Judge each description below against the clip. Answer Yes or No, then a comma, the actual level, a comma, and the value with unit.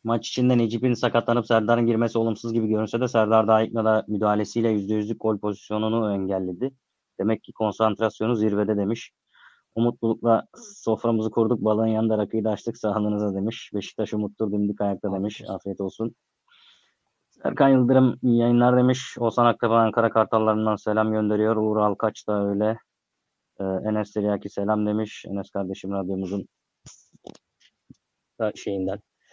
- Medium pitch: No, low, 110 Hz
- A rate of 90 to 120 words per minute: No, average, 135 wpm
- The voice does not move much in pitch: Yes, narrow, 1.8 semitones